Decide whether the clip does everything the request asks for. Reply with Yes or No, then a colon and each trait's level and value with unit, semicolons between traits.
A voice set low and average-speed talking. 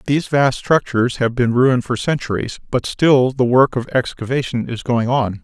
Yes: low, 125 Hz; average, 190 wpm